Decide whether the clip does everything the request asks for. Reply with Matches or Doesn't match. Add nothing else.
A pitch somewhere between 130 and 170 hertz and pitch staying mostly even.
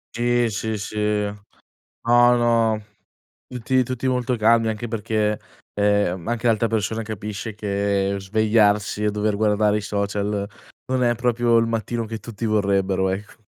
Doesn't match